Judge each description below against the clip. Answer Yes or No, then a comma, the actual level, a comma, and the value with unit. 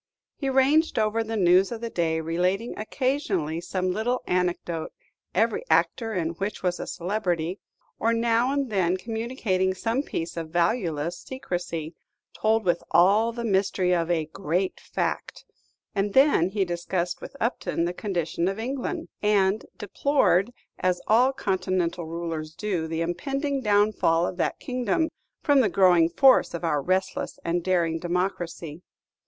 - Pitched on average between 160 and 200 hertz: Yes, high, 190 Hz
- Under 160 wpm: Yes, average, 150 wpm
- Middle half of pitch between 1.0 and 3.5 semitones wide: No, average, 4.8 semitones